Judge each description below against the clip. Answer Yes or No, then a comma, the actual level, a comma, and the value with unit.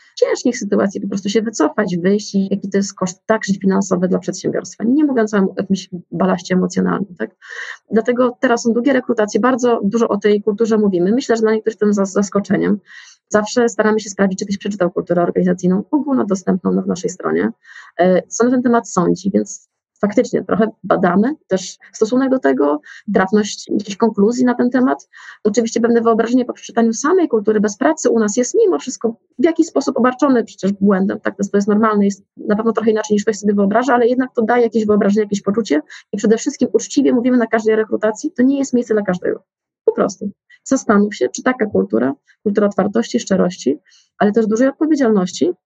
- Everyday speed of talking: No, fast, 195 wpm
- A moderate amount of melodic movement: Yes, average, 3.3 semitones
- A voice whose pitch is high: Yes, high, 215 Hz